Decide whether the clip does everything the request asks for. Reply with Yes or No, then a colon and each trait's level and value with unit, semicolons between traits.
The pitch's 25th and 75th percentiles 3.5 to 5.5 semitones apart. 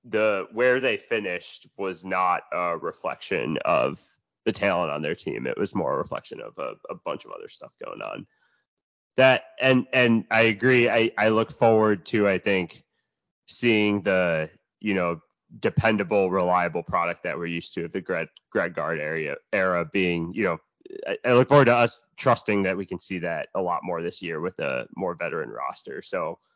Yes: average, 5.2 semitones